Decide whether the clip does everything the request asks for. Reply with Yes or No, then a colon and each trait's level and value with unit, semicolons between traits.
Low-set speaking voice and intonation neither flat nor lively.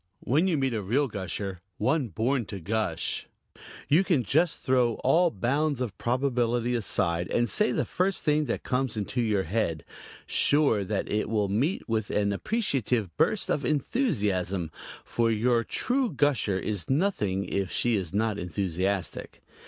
No: low, 115 Hz; wide, 5.9 semitones